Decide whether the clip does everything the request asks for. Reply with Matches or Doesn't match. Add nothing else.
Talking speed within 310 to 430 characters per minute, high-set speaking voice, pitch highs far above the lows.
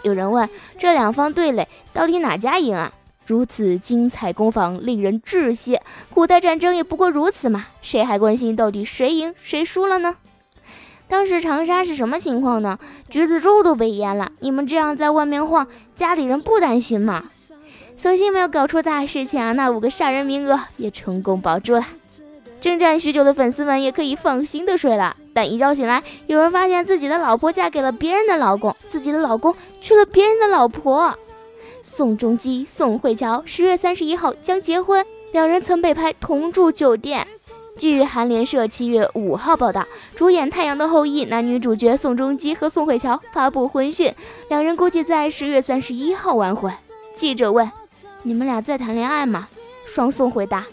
Doesn't match